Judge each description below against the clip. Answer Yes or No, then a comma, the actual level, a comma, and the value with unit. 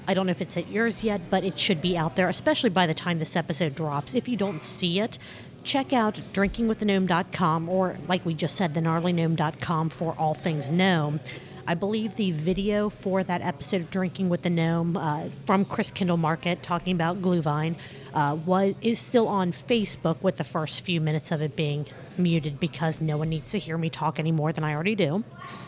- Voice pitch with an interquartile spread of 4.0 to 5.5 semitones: No, average, 3.2 semitones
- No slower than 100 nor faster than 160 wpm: No, fast, 205 wpm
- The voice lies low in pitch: No, medium, 175 Hz